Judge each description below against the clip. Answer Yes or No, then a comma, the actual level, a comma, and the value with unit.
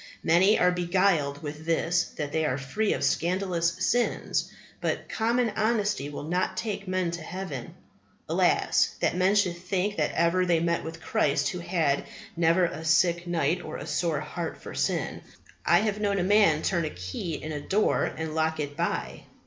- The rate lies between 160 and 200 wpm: Yes, average, 180 wpm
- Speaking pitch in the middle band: Yes, medium, 170 Hz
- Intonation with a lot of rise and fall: No, average, 3.2 semitones